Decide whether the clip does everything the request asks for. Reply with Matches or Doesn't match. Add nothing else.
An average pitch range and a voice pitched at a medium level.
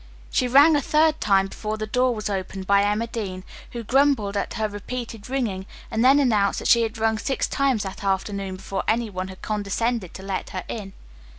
Doesn't match